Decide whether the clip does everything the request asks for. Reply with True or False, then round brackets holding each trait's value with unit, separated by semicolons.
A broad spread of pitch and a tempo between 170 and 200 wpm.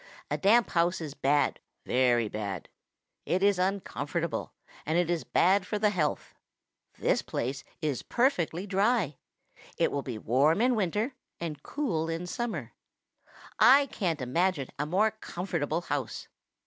False (5.7 semitones; 140 wpm)